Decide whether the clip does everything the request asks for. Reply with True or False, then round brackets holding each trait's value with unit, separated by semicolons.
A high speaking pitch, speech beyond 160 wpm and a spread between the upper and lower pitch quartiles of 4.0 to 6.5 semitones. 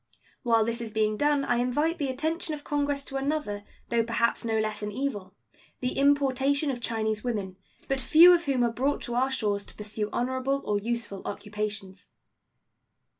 True (245 Hz; 175 wpm; 4.6 semitones)